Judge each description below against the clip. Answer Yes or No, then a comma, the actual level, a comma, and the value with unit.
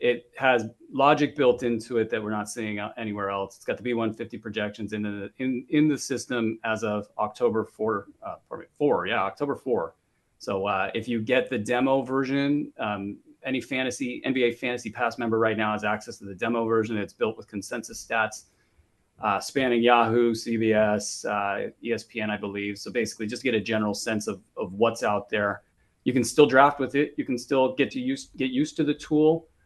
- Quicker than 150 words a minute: Yes, average, 200 wpm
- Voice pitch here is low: Yes, low, 115 Hz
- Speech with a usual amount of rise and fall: Yes, average, 3.7 semitones